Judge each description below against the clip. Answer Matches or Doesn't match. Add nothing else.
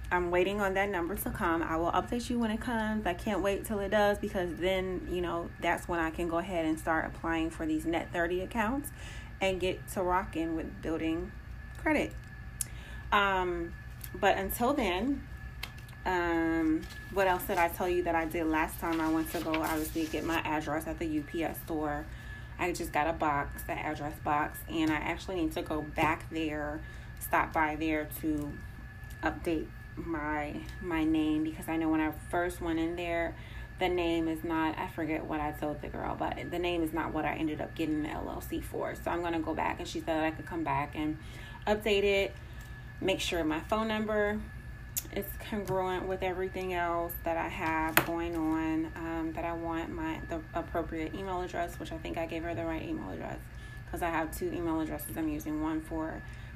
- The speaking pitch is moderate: Matches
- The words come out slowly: Doesn't match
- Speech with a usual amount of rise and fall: Doesn't match